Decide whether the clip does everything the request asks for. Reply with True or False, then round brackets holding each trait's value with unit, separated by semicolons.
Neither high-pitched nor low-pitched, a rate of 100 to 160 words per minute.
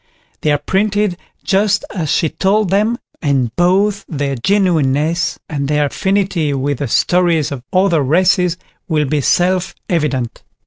True (170 Hz; 140 wpm)